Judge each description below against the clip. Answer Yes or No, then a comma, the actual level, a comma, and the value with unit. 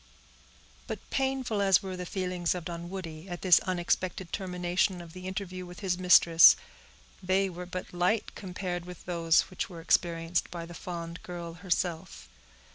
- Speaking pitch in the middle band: Yes, medium, 180 Hz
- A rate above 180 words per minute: No, average, 155 wpm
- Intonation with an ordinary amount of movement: No, narrow, 1.5 semitones